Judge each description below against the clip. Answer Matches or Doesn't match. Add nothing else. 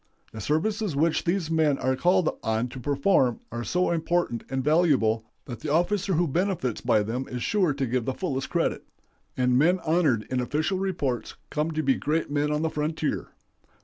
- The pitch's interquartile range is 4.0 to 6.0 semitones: Matches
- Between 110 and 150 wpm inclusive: Doesn't match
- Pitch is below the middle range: Doesn't match